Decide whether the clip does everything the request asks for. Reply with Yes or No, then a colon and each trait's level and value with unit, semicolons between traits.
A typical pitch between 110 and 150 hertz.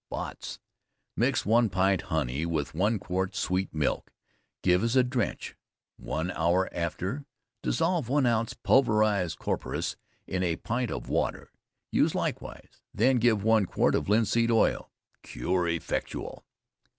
No: low, 100 Hz